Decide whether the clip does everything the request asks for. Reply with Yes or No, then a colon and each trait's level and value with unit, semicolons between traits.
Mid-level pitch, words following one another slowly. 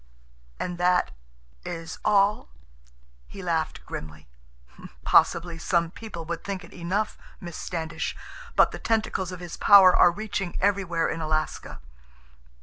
Yes: medium, 175 Hz; slow, 125 wpm